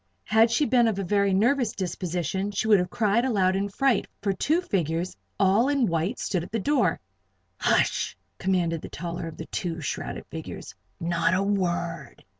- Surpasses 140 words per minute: Yes, average, 180 wpm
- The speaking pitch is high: Yes, high, 195 Hz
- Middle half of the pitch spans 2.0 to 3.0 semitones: No, average, 4.5 semitones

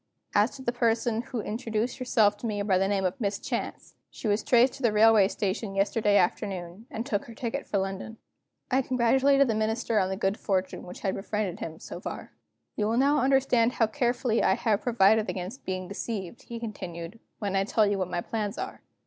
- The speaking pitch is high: Yes, high, 215 Hz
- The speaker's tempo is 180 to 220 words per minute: Yes, fast, 205 wpm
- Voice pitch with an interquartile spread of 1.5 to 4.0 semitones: Yes, average, 3.3 semitones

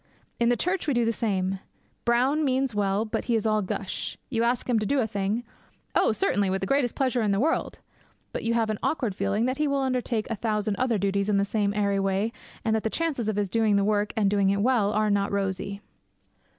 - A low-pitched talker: No, high, 215 Hz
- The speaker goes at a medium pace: No, fast, 240 wpm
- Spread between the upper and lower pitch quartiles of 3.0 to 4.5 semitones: Yes, average, 3.3 semitones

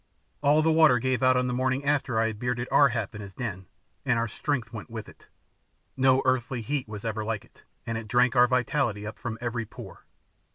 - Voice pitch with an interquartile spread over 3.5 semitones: No, narrow, 2.6 semitones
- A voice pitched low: Yes, low, 125 Hz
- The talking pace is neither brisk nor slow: No, fast, 220 wpm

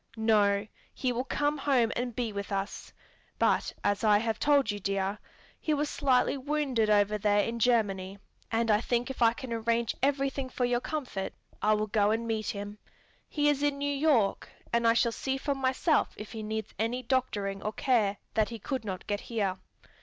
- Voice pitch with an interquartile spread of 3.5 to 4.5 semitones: Yes, average, 4.0 semitones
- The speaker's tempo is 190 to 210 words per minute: Yes, average, 195 wpm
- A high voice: Yes, high, 230 Hz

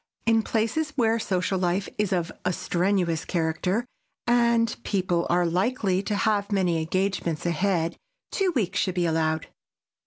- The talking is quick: No, average, 145 wpm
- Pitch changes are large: No, average, 4.0 semitones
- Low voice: No, high, 190 Hz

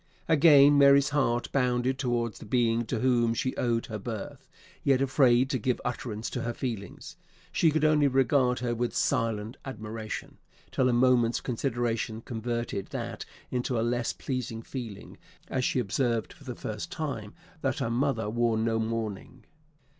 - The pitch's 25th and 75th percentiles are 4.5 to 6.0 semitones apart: No, narrow, 2.5 semitones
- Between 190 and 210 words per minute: No, average, 160 wpm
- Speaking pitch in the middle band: No, low, 120 Hz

